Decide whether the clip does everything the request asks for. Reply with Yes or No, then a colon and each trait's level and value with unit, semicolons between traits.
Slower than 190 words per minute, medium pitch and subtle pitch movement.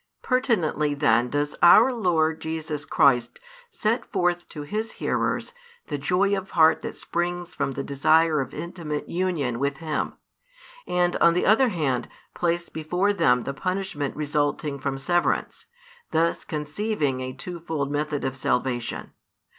No: average, 145 wpm; medium, 160 Hz; average, 3.9 semitones